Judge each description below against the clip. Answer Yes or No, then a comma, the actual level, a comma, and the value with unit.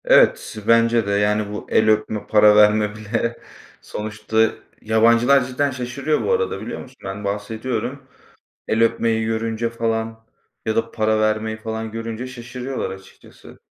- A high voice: No, low, 110 Hz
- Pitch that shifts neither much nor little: No, narrow, 1.8 semitones